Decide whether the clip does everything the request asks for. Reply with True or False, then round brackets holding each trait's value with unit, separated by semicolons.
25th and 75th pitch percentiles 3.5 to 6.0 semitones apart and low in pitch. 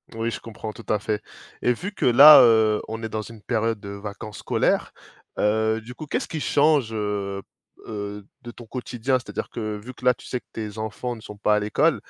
False (2.6 semitones; 110 Hz)